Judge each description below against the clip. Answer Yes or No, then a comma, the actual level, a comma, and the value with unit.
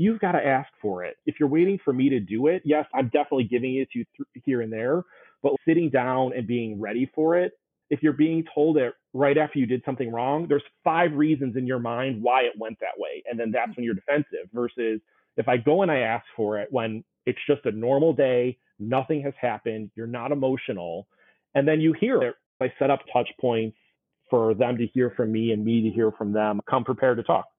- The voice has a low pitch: Yes, low, 130 Hz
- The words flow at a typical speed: No, fast, 235 wpm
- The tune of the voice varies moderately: Yes, average, 4.1 semitones